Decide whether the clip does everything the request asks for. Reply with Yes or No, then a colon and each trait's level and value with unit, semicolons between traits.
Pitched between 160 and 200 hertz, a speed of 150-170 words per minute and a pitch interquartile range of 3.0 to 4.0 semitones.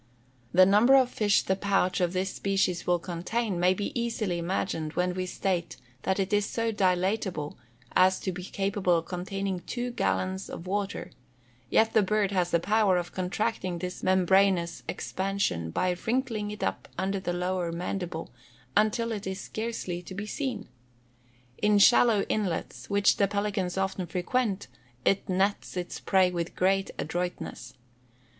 No: high, 190 Hz; average, 155 wpm; narrow, 2.4 semitones